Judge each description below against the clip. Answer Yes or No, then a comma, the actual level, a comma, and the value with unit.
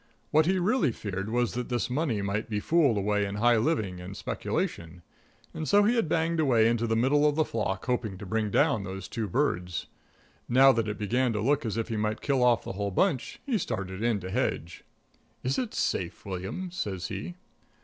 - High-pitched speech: No, low, 115 Hz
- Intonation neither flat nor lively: No, wide, 6.0 semitones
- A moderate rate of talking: No, fast, 210 wpm